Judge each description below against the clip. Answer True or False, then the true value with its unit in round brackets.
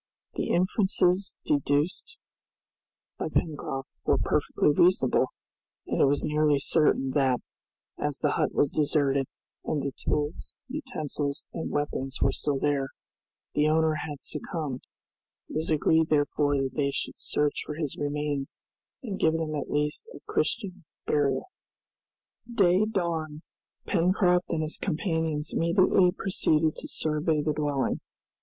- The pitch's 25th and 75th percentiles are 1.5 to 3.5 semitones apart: True (2.7 semitones)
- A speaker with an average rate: False (130 wpm)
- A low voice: False (150 Hz)